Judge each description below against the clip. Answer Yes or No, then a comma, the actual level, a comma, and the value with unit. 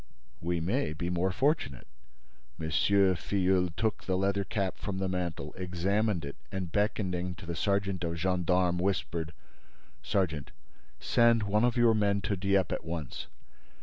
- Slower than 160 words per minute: Yes, average, 150 wpm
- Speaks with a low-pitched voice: Yes, very low, 95 Hz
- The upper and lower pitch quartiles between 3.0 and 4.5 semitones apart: No, narrow, 2.6 semitones